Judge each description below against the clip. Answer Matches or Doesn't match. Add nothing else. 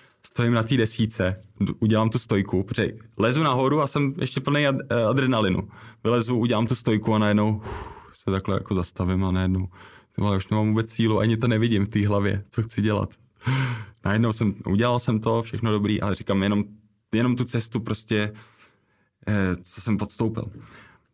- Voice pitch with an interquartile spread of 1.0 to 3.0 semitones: Matches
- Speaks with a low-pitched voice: Matches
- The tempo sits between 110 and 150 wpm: Doesn't match